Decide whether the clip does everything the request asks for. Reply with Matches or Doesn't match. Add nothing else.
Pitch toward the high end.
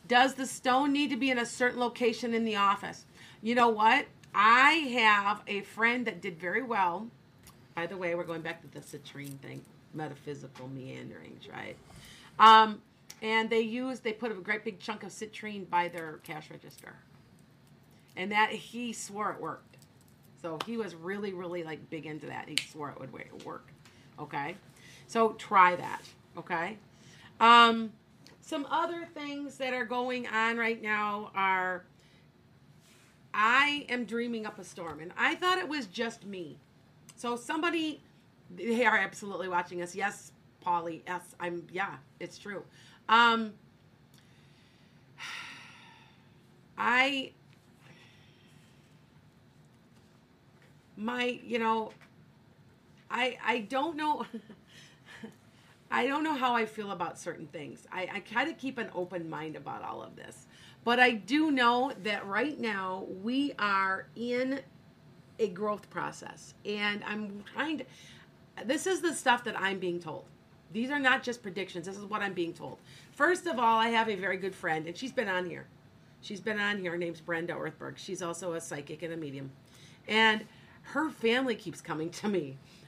Matches